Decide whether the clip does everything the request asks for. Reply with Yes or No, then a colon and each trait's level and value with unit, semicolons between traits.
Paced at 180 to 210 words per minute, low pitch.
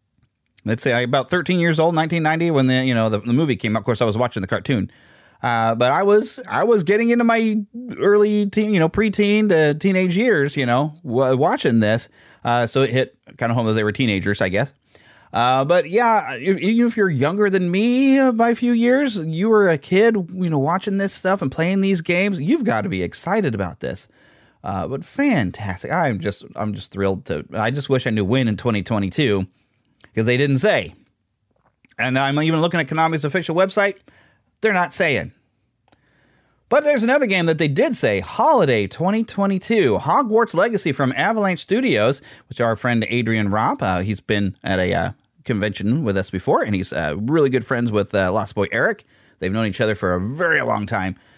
No: fast, 205 wpm; medium, 145 Hz